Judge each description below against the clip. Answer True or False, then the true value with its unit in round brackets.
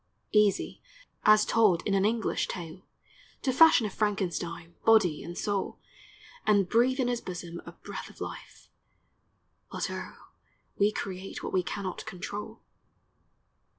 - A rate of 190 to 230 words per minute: False (135 wpm)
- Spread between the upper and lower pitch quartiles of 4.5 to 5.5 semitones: False (3.4 semitones)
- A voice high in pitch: True (200 Hz)